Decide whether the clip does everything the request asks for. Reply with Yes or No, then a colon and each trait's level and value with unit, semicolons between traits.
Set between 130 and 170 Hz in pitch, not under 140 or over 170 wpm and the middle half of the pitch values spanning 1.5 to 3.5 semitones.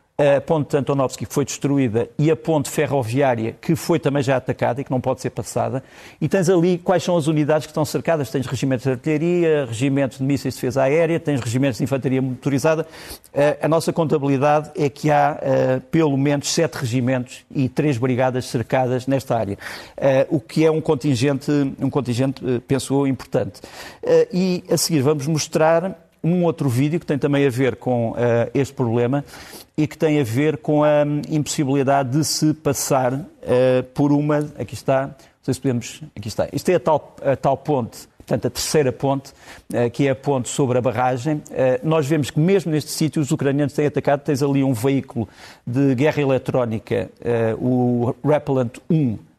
No: medium, 140 Hz; fast, 185 wpm; average, 3.0 semitones